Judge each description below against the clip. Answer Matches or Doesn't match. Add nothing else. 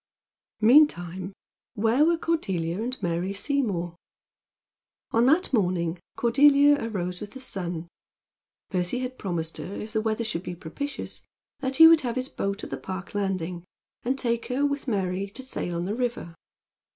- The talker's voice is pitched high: Matches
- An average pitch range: Doesn't match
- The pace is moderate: Matches